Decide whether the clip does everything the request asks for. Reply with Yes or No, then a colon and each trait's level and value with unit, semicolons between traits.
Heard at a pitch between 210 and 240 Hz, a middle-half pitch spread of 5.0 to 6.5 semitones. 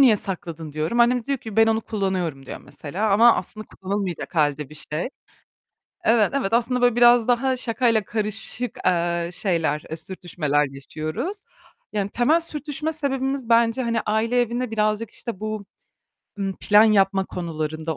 Yes: high, 215 Hz; wide, 5.6 semitones